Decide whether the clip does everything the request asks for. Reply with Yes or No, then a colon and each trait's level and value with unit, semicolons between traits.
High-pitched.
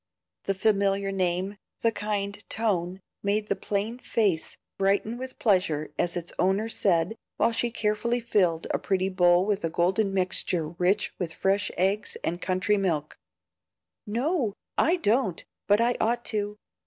Yes: high, 200 Hz